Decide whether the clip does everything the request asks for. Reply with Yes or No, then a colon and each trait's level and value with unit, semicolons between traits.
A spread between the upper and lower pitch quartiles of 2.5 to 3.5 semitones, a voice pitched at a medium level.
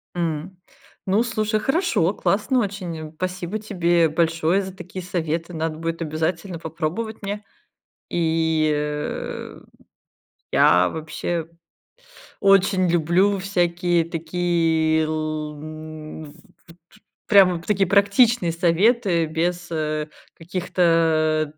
Yes: average, 3.2 semitones; medium, 170 Hz